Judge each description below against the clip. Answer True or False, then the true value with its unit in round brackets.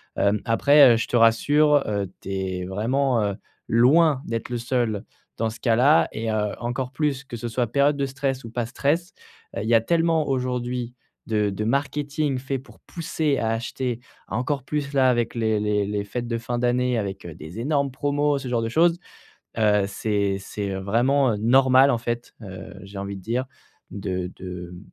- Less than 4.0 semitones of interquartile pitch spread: False (4.5 semitones)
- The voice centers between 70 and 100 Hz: False (120 Hz)